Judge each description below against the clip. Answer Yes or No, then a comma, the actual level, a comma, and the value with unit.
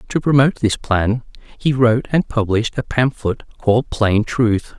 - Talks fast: No, average, 165 wpm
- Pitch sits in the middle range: No, low, 120 Hz